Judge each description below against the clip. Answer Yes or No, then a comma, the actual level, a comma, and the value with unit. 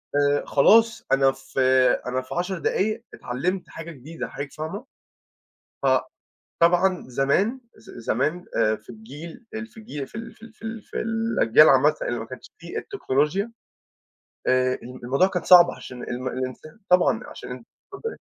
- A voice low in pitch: No, medium, 165 Hz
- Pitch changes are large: Yes, wide, 8.5 semitones